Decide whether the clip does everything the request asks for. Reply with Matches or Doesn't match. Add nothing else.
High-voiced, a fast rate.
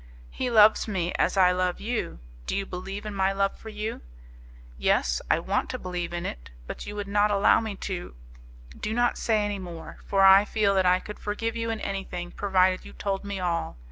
Matches